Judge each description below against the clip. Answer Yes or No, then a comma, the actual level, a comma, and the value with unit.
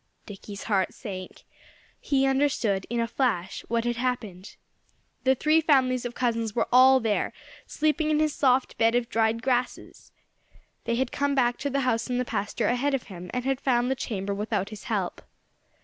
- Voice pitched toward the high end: Yes, high, 245 Hz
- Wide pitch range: No, average, 3.3 semitones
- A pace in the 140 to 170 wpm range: No, average, 180 wpm